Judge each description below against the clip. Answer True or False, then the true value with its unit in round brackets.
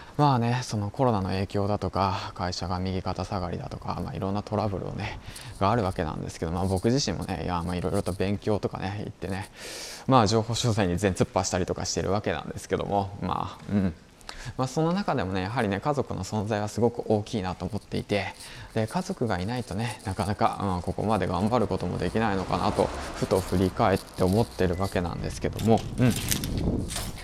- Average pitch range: True (3.6 semitones)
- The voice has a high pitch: False (100 Hz)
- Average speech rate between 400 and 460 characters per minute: True (420 characters per minute)